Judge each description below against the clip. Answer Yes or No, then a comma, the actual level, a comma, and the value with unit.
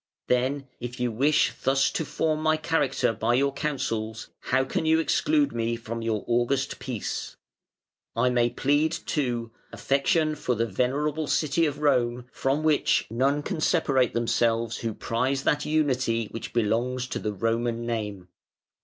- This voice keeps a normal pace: Yes, average, 155 wpm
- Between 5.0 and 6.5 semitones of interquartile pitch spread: No, average, 4.0 semitones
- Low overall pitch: Yes, low, 125 Hz